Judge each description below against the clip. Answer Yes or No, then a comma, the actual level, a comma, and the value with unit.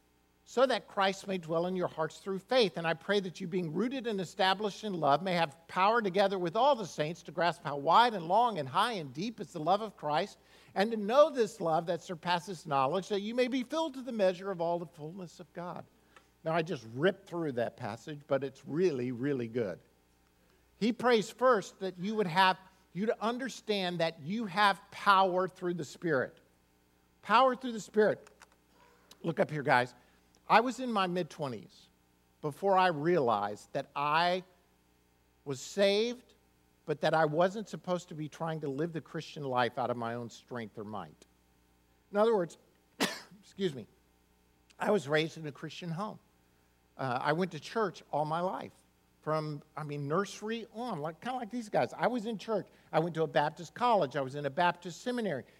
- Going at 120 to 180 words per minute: No, average, 195 wpm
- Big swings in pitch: Yes, wide, 6.4 semitones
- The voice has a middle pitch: Yes, medium, 175 Hz